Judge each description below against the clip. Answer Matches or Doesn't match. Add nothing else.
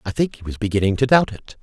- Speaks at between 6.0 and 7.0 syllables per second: Matches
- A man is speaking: Matches